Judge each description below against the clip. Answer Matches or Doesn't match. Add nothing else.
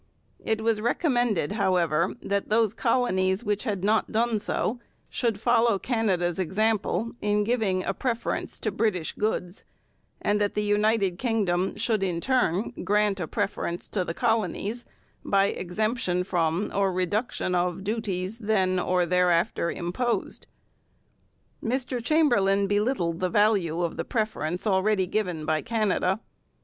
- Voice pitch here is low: Doesn't match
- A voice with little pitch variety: Doesn't match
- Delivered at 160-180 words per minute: Doesn't match